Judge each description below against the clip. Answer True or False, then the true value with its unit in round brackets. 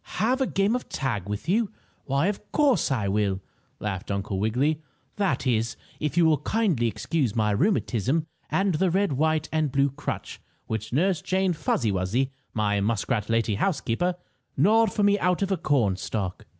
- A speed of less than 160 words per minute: False (170 wpm)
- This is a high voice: False (140 Hz)